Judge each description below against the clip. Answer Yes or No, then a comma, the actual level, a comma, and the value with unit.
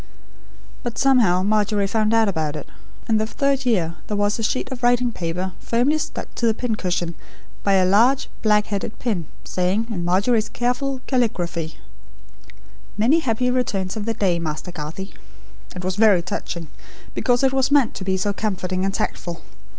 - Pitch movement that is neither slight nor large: Yes, average, 4.8 semitones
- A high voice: Yes, high, 210 Hz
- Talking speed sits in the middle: Yes, average, 170 wpm